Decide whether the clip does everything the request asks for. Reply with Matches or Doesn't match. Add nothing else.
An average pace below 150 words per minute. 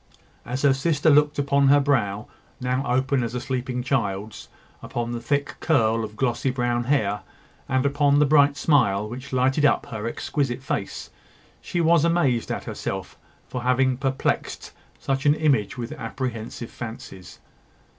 Doesn't match